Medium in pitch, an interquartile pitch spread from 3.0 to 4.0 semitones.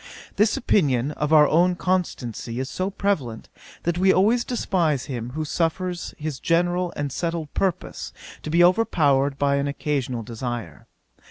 No: medium, 155 Hz; average, 4.8 semitones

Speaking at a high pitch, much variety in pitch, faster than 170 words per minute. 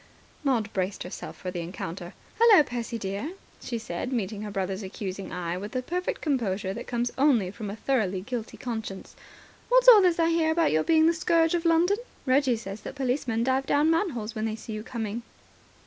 Yes: high, 235 Hz; wide, 7.2 semitones; average, 195 wpm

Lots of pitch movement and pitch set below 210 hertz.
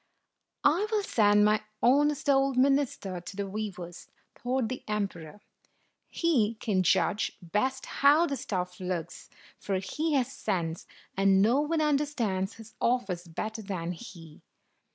No: wide, 6.4 semitones; high, 215 Hz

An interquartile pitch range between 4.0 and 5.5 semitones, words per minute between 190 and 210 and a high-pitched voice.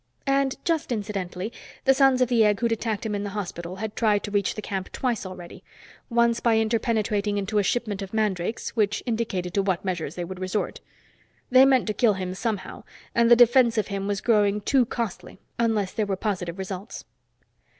No: average, 3.3 semitones; average, 195 wpm; high, 210 Hz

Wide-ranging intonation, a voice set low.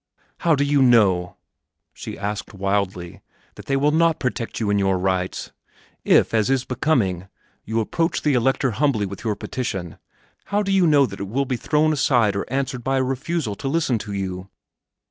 Yes: wide, 6.0 semitones; low, 120 Hz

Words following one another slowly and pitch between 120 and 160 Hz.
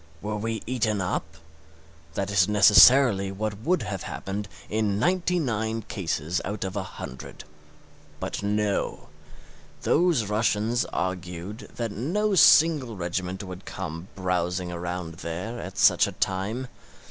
No: slow, 130 wpm; low, 105 Hz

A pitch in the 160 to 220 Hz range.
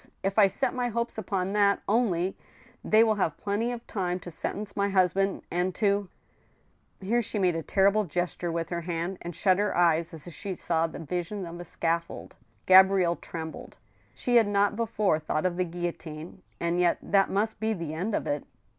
Yes: medium, 185 Hz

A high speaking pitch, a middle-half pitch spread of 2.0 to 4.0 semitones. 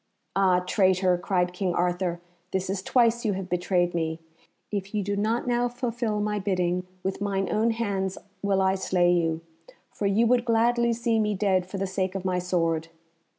Yes: high, 195 Hz; average, 3.0 semitones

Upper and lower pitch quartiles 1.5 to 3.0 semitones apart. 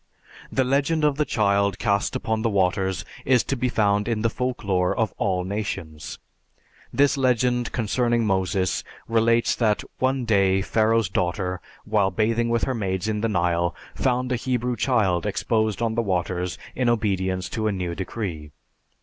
No: average, 3.9 semitones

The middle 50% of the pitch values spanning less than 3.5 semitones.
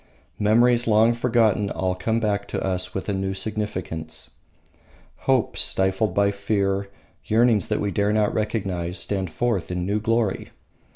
Yes: narrow, 2.6 semitones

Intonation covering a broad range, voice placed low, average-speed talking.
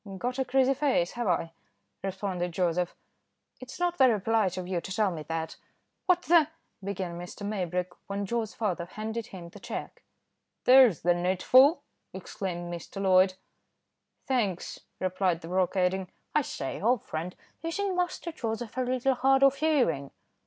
No: wide, 6.2 semitones; high, 200 Hz; average, 160 wpm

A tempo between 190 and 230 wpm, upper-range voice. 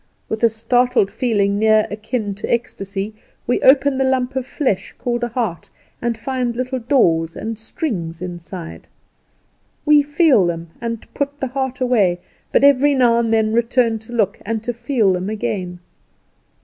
No: average, 160 wpm; high, 230 Hz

